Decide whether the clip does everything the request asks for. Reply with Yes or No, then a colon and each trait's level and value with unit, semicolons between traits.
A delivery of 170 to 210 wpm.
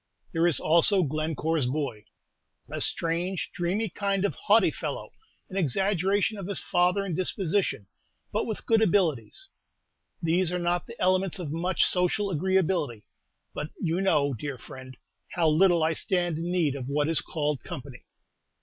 No: average, 155 wpm